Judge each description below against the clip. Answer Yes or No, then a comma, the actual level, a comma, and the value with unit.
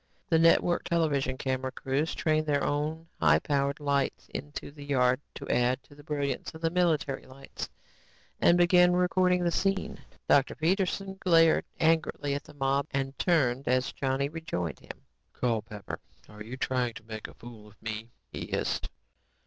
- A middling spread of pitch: Yes, average, 4.2 semitones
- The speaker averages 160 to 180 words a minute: Yes, average, 165 wpm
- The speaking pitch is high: No, medium, 140 Hz